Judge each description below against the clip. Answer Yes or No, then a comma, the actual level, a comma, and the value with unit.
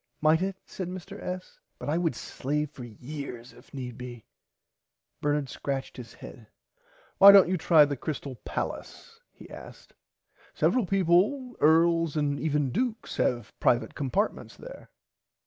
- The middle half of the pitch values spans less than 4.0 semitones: No, wide, 5.6 semitones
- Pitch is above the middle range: No, medium, 155 Hz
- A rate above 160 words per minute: No, average, 145 wpm